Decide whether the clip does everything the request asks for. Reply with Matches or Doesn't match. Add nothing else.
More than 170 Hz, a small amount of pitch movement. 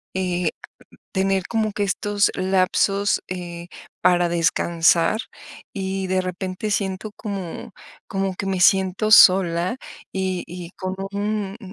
Matches